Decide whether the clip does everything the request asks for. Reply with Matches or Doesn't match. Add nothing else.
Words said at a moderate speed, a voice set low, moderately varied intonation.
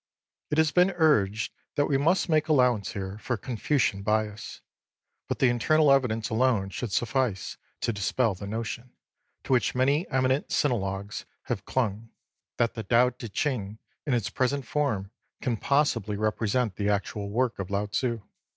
Matches